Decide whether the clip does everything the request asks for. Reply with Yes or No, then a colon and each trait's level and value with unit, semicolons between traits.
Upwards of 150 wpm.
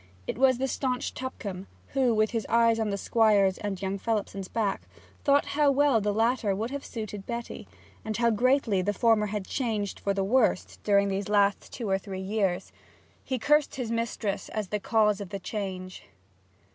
Yes: average, 185 wpm